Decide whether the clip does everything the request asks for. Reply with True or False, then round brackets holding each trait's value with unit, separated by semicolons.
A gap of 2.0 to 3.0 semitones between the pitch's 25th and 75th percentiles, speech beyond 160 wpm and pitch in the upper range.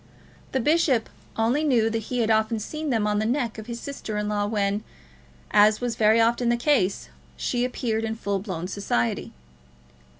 True (2.6 semitones; 180 wpm; 225 Hz)